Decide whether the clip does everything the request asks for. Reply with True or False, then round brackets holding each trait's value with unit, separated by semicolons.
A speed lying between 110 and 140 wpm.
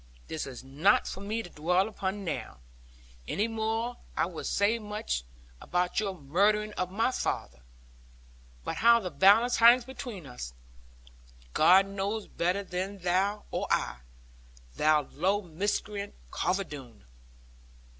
True (135 wpm)